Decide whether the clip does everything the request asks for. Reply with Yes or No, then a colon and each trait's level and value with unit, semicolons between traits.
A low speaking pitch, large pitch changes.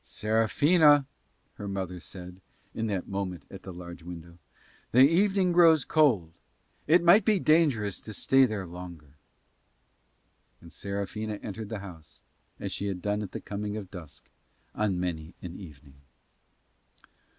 Yes: low, 100 Hz; wide, 6.6 semitones